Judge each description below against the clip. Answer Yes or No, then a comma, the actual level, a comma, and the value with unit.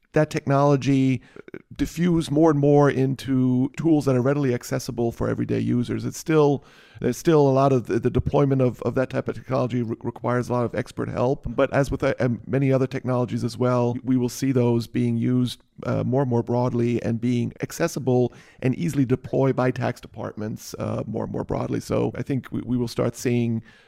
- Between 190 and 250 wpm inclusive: Yes, average, 200 wpm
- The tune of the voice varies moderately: No, narrow, 2.2 semitones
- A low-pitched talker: Yes, low, 125 Hz